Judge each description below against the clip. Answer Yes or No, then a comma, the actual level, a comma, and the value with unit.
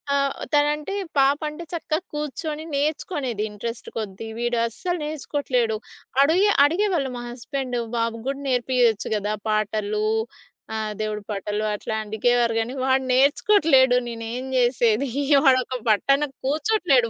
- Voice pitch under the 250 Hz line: No, very high, 255 Hz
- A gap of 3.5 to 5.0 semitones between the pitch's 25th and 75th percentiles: Yes, average, 4.5 semitones